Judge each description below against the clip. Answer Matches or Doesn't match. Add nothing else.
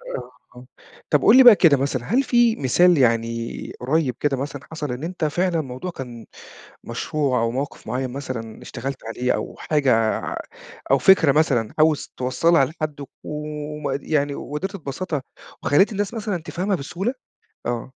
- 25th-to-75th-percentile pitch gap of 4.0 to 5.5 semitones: Matches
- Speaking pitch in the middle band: Matches